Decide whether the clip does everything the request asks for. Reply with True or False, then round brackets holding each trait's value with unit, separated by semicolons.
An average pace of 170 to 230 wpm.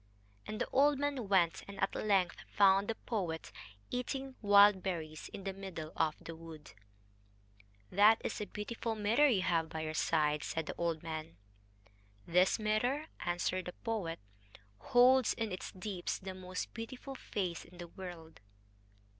False (155 wpm)